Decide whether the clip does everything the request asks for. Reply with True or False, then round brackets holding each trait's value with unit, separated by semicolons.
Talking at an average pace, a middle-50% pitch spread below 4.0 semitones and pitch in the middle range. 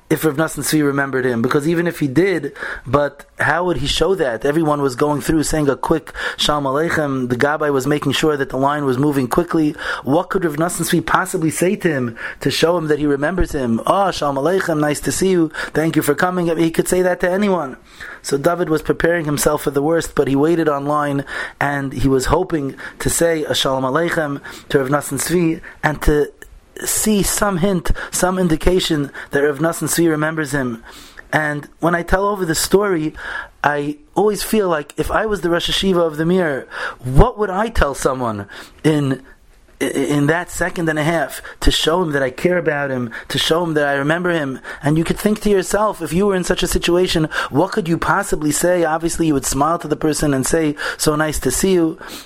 False (210 wpm; 3.3 semitones; 160 Hz)